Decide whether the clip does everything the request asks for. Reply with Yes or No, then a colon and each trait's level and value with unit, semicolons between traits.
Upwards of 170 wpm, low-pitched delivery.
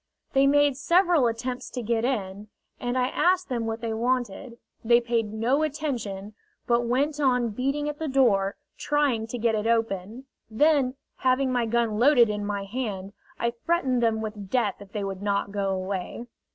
No: average, 180 wpm; high, 235 Hz